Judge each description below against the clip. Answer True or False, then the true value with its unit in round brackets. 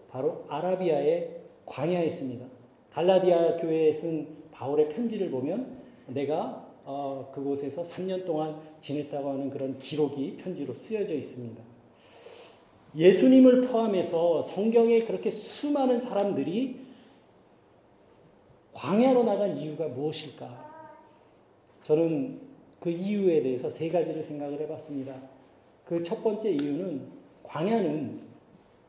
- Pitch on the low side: False (165 Hz)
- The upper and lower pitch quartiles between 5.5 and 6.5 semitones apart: False (7.6 semitones)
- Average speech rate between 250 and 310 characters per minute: True (260 characters per minute)